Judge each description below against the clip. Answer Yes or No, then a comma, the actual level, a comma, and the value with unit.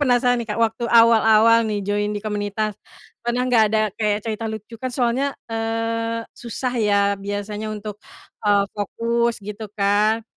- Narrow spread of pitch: Yes, narrow, 1.9 semitones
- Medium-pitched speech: No, high, 220 Hz